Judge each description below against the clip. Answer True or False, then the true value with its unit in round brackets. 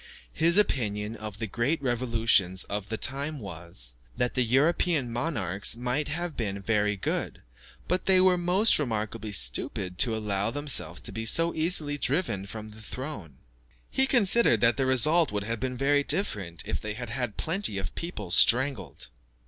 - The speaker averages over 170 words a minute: False (165 wpm)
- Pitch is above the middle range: False (120 Hz)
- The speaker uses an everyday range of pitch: False (6.3 semitones)